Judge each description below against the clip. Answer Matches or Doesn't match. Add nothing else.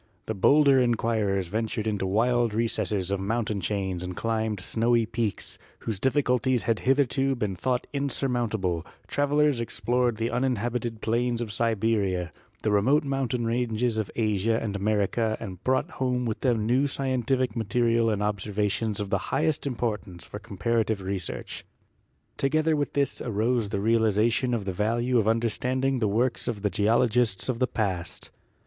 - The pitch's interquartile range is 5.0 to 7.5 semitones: Doesn't match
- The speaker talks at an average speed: Matches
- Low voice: Matches